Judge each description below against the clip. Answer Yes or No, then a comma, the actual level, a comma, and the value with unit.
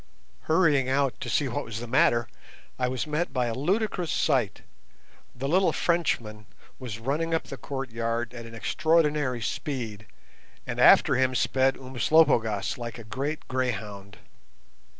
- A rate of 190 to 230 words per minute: No, average, 145 wpm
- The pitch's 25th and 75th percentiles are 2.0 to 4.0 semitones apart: No, average, 4.5 semitones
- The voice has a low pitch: Yes, low, 130 Hz